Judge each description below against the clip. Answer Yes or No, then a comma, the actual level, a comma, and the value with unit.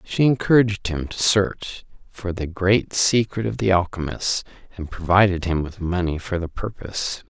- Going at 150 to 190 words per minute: Yes, average, 165 wpm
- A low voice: Yes, very low, 95 Hz